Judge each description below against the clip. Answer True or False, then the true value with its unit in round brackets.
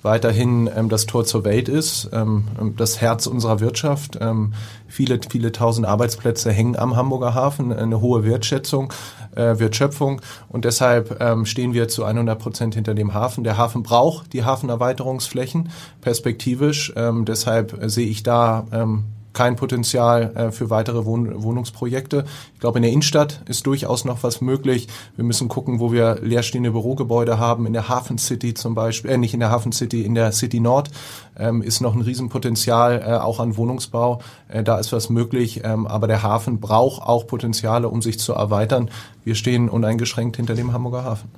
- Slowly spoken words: False (170 wpm)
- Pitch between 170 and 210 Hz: False (120 Hz)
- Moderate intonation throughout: False (1.7 semitones)